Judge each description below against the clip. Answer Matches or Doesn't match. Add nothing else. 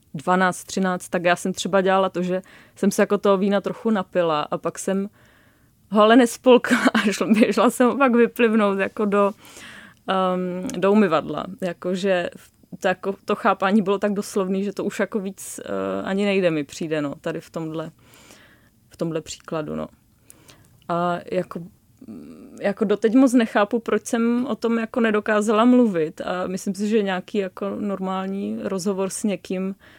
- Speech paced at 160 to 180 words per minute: Matches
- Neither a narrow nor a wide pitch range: Matches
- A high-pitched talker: Matches